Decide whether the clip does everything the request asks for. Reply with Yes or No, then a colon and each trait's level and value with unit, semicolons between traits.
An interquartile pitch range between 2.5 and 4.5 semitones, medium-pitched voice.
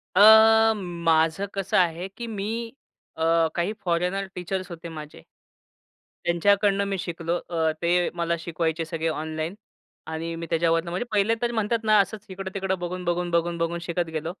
Yes: average, 2.9 semitones; medium, 175 Hz